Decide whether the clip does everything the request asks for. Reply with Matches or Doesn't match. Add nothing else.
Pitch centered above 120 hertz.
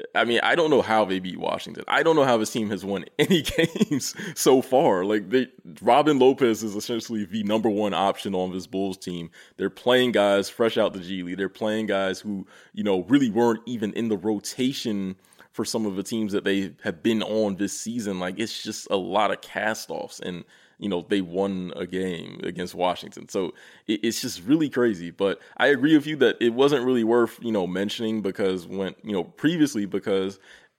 Doesn't match